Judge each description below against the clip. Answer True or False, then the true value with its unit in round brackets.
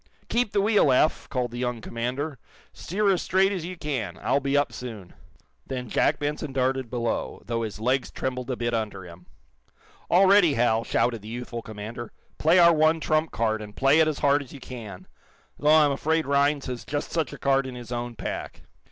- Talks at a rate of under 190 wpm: False (205 wpm)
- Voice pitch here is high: False (130 Hz)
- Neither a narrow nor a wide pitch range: True (4.6 semitones)